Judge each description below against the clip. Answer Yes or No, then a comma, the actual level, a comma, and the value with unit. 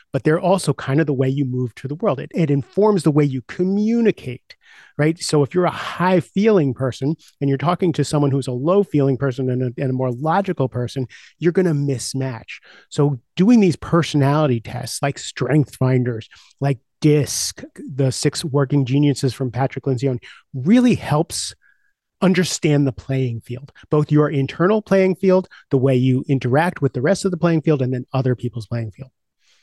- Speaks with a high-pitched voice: No, medium, 140 Hz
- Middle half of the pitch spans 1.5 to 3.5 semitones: No, average, 4.7 semitones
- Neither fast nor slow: Yes, average, 180 wpm